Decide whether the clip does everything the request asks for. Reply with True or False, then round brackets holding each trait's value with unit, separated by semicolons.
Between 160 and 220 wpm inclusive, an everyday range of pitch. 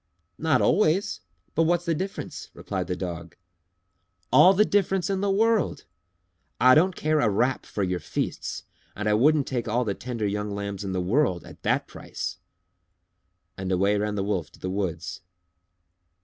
False (170 wpm; 8.9 semitones)